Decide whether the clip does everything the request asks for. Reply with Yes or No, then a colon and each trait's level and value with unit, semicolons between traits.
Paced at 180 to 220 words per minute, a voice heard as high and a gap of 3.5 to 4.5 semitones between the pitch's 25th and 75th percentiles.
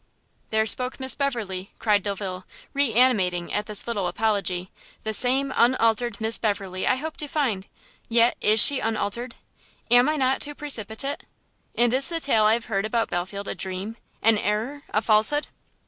No: average, 170 wpm; high, 225 Hz; average, 4.1 semitones